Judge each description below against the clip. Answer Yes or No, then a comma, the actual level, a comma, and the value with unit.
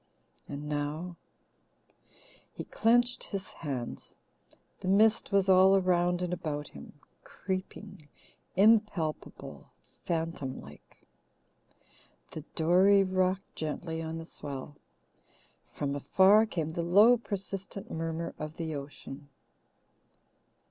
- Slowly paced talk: Yes, slow, 105 wpm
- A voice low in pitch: No, medium, 175 Hz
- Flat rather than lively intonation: No, average, 4.2 semitones